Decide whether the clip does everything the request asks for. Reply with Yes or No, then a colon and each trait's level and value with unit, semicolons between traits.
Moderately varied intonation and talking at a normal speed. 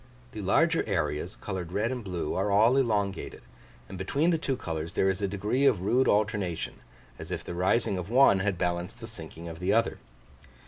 Yes: average, 4.4 semitones; average, 195 wpm